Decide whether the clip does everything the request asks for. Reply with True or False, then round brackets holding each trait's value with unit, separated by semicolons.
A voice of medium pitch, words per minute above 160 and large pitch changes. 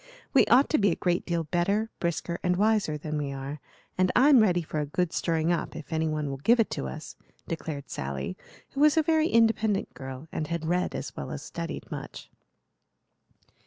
True (170 Hz; 200 wpm; 6.0 semitones)